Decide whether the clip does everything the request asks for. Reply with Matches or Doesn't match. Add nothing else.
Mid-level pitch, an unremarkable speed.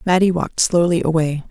Matches